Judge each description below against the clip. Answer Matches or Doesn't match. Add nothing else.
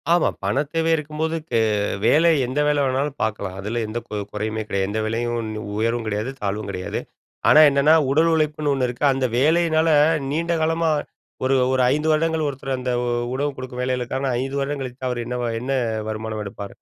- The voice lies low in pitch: Matches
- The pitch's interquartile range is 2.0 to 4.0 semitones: Doesn't match